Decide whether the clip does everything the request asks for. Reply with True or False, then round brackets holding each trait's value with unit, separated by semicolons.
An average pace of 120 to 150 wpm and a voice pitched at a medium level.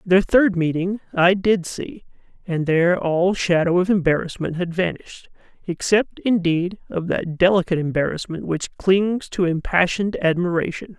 True (135 wpm; 180 Hz)